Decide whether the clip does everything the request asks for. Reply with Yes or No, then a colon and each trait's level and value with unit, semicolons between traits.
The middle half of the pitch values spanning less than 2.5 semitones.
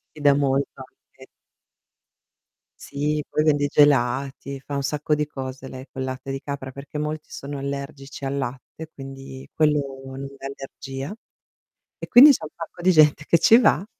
Yes: narrow, 1.9 semitones